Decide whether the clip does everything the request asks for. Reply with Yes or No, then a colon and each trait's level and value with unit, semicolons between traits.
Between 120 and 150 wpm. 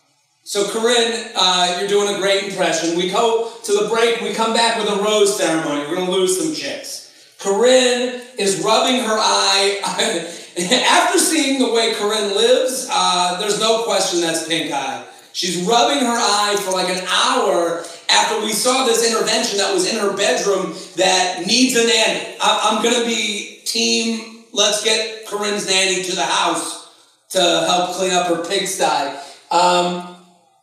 No: average, 165 wpm